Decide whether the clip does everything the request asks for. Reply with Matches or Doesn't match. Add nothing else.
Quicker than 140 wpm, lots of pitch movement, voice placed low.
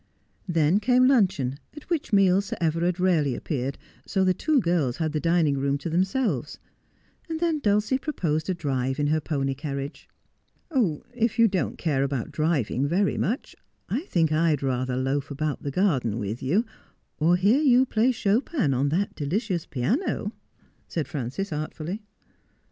Doesn't match